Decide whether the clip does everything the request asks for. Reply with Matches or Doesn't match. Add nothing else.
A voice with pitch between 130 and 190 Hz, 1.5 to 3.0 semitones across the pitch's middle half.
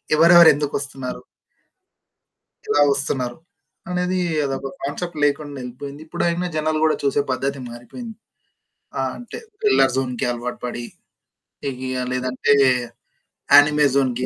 Doesn't match